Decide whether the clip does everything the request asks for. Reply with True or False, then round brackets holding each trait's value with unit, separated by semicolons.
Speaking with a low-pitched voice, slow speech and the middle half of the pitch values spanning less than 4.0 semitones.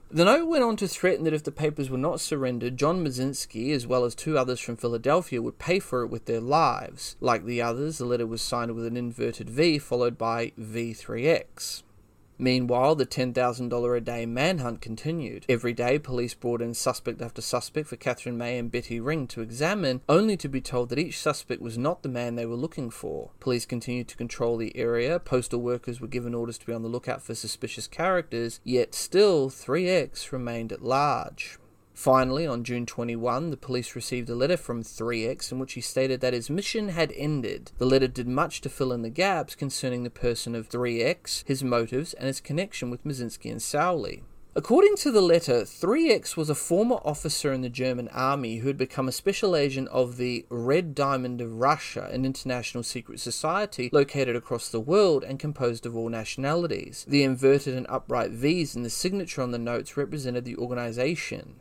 False (125 Hz; 200 wpm; 3.5 semitones)